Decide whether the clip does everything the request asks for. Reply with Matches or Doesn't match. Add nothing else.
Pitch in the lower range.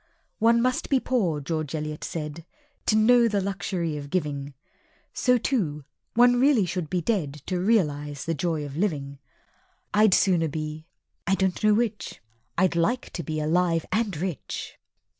Doesn't match